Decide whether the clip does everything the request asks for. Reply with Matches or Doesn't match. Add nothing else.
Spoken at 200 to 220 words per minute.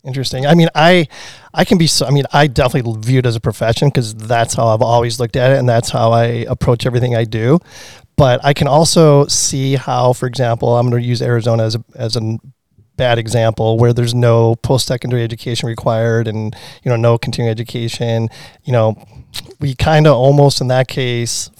Matches